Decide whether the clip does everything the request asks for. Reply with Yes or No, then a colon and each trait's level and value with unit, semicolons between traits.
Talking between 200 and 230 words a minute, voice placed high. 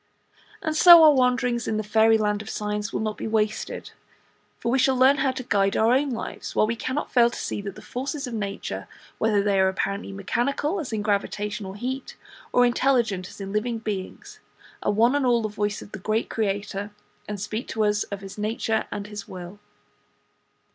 Yes: fast, 205 wpm; high, 215 Hz